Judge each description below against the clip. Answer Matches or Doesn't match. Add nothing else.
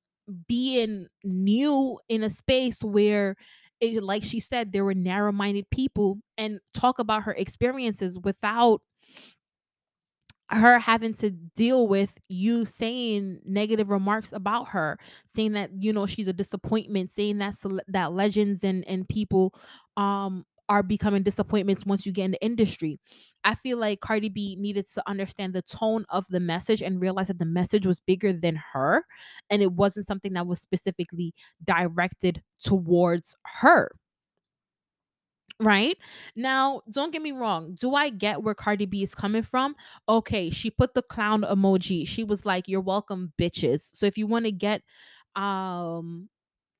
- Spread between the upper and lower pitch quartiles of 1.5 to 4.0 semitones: Matches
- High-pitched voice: Matches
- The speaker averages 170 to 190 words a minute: Doesn't match